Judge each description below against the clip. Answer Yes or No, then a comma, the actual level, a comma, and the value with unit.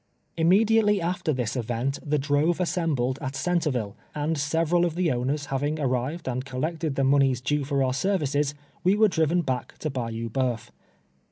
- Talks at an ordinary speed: Yes, average, 170 wpm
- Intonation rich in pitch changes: No, average, 4.3 semitones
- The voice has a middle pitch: Yes, medium, 145 Hz